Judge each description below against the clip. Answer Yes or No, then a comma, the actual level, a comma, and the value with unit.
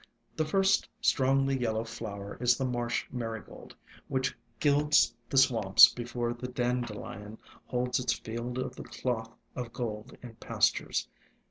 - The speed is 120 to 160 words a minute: Yes, average, 140 wpm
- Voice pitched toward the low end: Yes, low, 120 Hz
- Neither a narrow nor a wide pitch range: No, narrow, 2.3 semitones